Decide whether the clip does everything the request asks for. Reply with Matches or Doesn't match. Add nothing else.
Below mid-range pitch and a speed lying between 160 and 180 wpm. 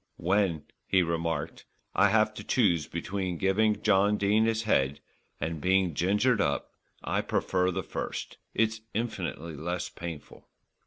Doesn't match